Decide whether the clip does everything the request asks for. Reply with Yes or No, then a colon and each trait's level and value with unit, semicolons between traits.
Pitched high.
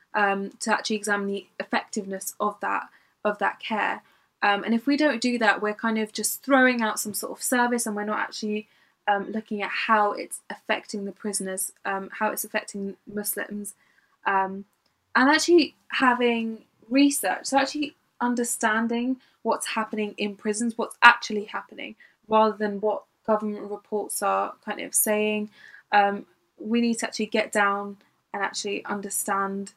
Yes: high, 215 Hz